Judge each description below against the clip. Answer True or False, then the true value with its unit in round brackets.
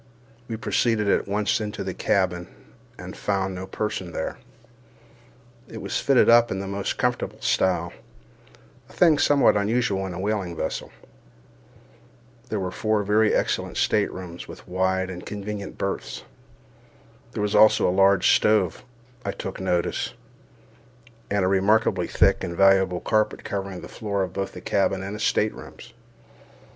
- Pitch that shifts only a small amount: True (2.1 semitones)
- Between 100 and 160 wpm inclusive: True (145 wpm)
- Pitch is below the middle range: True (100 Hz)